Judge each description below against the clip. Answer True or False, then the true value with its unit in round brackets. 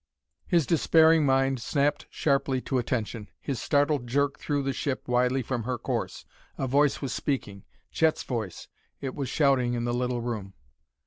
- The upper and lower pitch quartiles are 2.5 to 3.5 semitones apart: True (2.8 semitones)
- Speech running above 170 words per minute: False (165 wpm)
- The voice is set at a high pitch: False (130 Hz)